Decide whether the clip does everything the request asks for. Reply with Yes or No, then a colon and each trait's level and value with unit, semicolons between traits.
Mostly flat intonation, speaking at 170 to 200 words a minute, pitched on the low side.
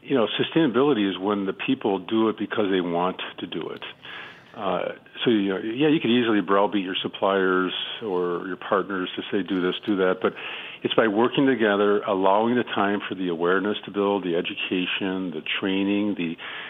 Yes: narrow, 2.1 semitones; average, 190 wpm; low, 100 Hz